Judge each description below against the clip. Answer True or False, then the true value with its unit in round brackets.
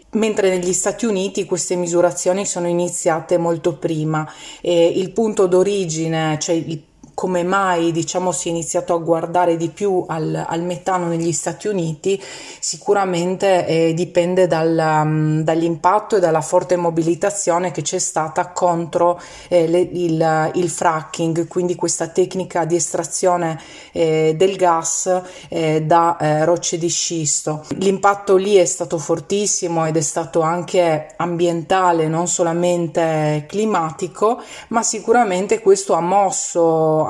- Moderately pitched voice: True (175 Hz)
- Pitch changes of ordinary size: False (2.0 semitones)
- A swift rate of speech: False (135 wpm)